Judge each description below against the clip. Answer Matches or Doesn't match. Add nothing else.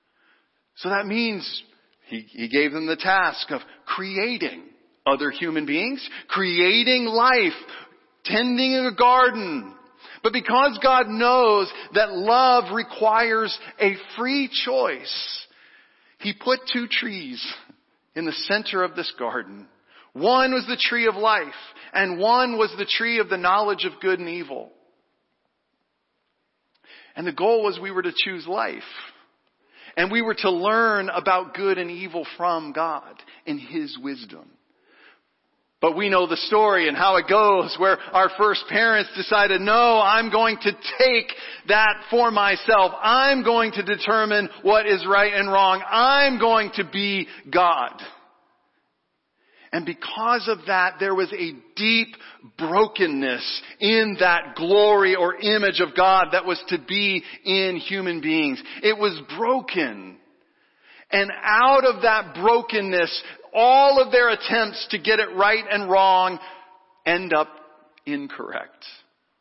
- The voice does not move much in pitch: Doesn't match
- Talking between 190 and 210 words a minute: Doesn't match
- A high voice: Matches